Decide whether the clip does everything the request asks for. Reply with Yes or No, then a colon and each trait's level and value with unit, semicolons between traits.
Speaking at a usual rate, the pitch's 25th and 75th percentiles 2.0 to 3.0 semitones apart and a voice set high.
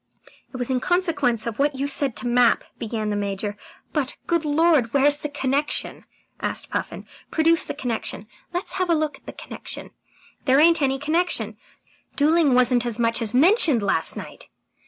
No: average, 180 wpm; average, 4.7 semitones; very high, 275 Hz